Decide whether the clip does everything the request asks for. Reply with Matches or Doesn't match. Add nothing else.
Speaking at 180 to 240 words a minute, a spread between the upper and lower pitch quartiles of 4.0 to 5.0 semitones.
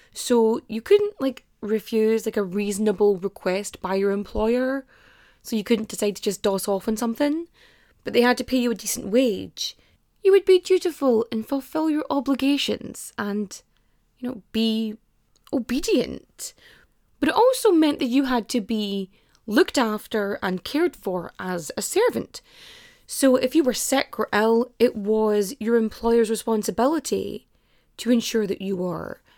Doesn't match